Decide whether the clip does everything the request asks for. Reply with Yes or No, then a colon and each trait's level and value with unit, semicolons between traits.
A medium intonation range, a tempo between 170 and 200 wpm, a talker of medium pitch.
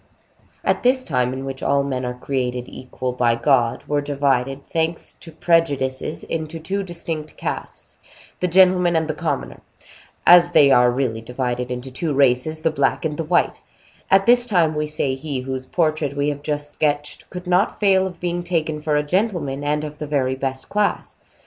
Yes: average, 4.2 semitones; average, 175 wpm; medium, 150 Hz